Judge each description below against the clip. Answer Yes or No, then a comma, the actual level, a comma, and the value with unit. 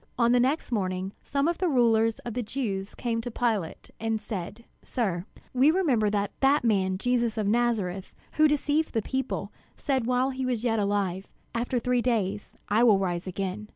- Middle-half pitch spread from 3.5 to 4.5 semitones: Yes, average, 3.9 semitones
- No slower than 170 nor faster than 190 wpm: Yes, average, 185 wpm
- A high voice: Yes, high, 230 Hz